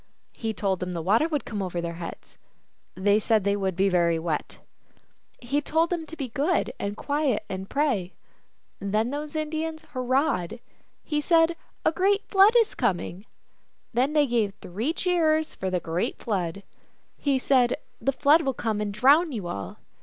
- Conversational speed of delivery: Yes, average, 180 wpm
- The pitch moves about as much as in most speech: No, wide, 7.9 semitones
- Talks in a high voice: Yes, high, 240 Hz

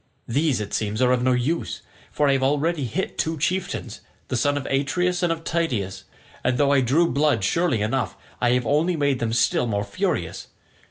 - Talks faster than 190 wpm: Yes, average, 200 wpm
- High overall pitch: No, low, 135 Hz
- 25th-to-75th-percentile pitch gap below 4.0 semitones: No, average, 4.7 semitones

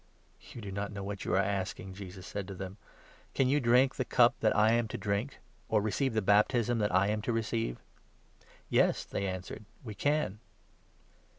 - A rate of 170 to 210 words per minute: Yes, fast, 205 wpm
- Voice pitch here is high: No, low, 105 Hz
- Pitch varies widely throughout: No, average, 3.2 semitones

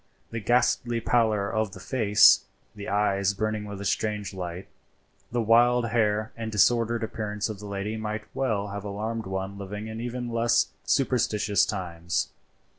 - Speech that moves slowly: No, average, 155 wpm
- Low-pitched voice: Yes, low, 105 Hz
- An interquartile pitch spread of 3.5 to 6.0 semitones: No, narrow, 2.4 semitones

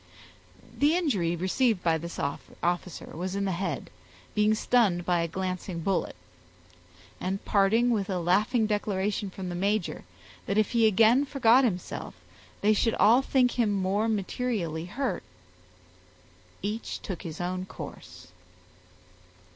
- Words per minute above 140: No, slow, 135 wpm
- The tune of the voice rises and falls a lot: No, average, 3.9 semitones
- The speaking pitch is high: Yes, high, 200 Hz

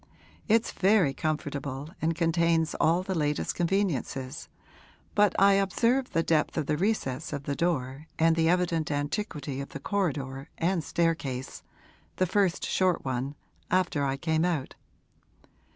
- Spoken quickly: No, average, 140 wpm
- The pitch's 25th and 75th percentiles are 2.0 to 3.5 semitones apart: No, average, 4.3 semitones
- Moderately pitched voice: Yes, medium, 165 Hz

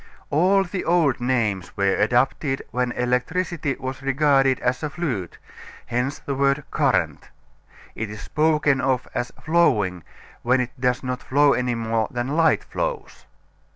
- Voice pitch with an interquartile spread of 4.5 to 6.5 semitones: No, average, 3.6 semitones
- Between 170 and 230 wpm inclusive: No, average, 145 wpm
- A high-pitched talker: No, low, 130 Hz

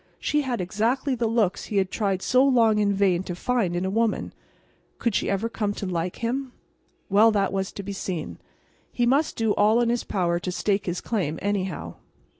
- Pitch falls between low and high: No, high, 205 Hz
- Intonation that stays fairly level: No, average, 3.7 semitones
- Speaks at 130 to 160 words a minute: No, fast, 205 wpm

